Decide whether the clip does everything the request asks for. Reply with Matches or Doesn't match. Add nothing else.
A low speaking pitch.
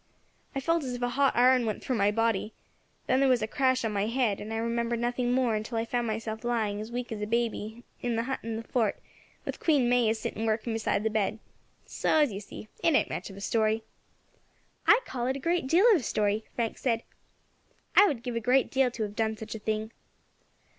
Doesn't match